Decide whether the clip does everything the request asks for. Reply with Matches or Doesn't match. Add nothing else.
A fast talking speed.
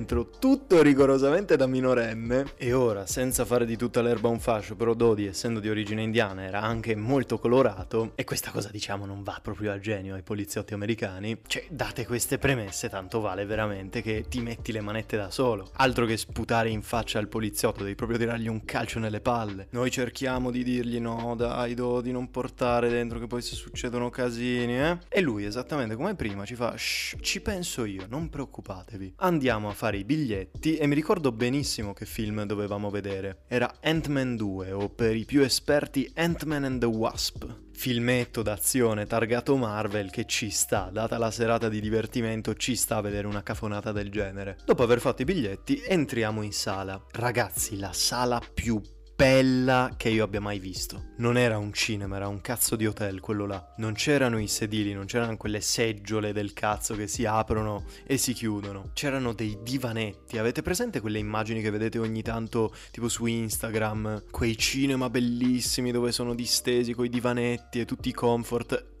Matches